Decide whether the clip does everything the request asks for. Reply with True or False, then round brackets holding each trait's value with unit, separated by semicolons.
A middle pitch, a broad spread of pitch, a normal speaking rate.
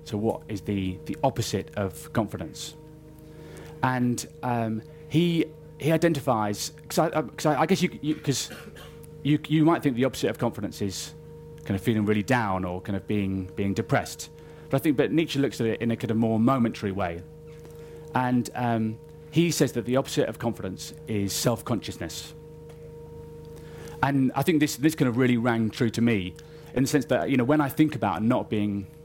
False (130 Hz; 6.1 semitones; 190 wpm)